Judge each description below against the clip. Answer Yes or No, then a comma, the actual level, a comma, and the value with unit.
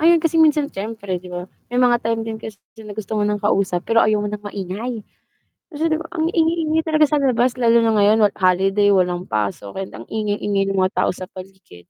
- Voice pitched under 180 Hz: No, high, 210 Hz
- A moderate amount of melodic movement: Yes, average, 4.6 semitones